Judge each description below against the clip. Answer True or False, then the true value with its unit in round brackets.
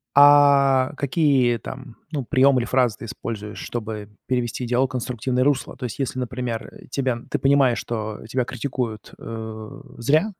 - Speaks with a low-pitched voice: True (125 Hz)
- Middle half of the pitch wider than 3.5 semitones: False (2.9 semitones)